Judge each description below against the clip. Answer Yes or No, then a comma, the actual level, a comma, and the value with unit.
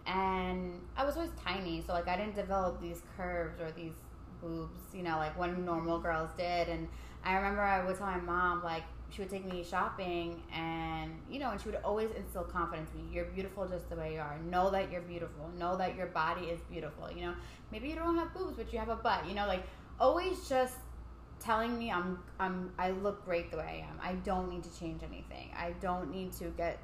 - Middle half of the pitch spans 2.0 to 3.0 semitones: Yes, narrow, 2.4 semitones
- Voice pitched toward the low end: No, medium, 180 Hz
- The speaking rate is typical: No, fast, 230 wpm